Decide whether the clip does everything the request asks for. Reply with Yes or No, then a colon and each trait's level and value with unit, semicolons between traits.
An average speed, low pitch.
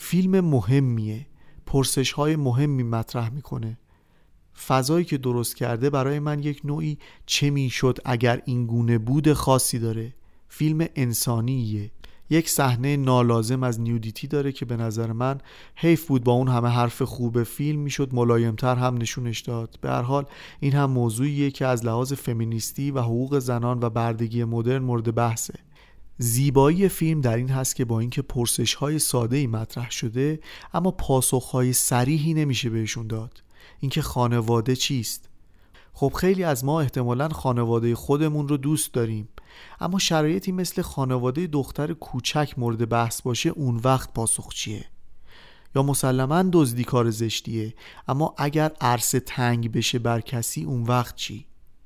Yes: average, 145 wpm; low, 130 Hz